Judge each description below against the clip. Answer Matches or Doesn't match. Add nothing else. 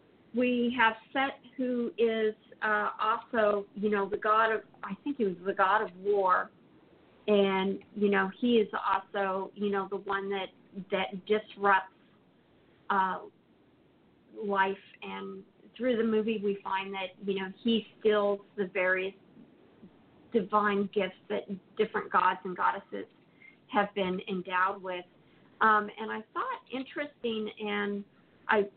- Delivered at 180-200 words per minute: Doesn't match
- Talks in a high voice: Matches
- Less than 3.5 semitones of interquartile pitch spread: Matches